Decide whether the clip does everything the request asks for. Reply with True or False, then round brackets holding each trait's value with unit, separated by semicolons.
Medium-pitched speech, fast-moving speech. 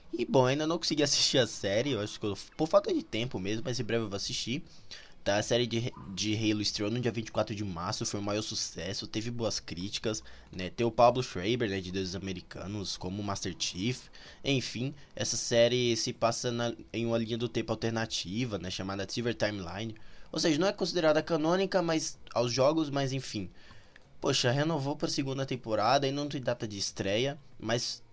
False (115 Hz; 200 wpm)